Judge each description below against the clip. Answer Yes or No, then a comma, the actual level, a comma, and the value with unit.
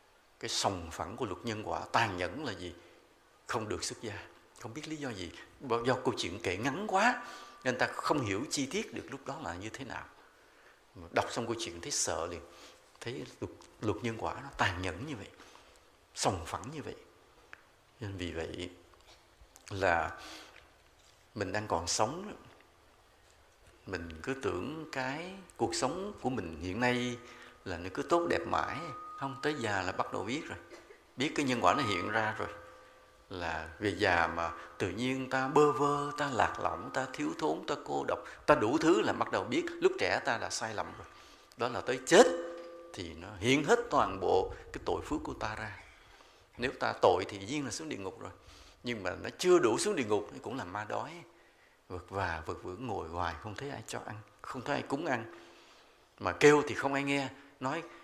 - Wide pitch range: Yes, wide, 8.0 semitones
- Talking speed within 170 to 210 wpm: Yes, average, 200 wpm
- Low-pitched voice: Yes, low, 115 Hz